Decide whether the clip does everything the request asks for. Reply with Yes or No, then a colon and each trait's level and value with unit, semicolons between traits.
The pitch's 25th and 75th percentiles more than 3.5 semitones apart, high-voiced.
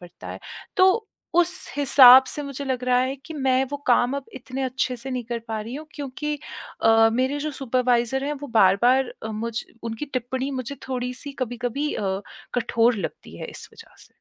No: average, 2.8 semitones; very high, 255 Hz